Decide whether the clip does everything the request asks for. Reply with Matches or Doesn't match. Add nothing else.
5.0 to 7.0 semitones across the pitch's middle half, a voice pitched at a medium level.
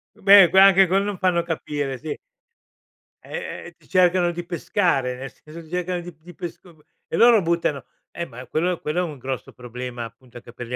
Matches